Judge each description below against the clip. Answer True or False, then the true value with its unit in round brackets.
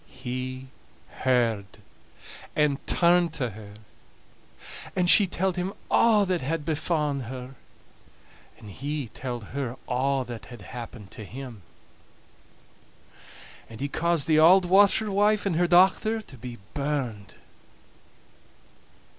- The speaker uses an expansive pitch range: True (6.2 semitones)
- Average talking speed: False (115 wpm)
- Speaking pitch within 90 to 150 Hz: True (140 Hz)